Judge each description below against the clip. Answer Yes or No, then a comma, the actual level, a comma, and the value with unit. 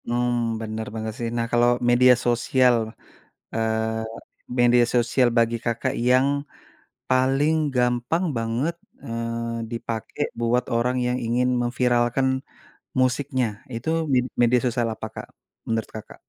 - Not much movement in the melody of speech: Yes, narrow, 1.4 semitones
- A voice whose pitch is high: No, low, 120 Hz